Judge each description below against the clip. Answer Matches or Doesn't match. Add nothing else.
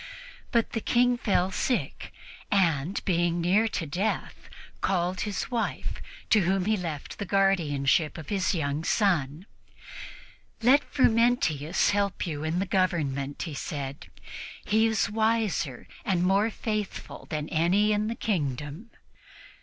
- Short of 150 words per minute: Matches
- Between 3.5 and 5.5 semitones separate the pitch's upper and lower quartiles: Matches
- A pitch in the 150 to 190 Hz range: Matches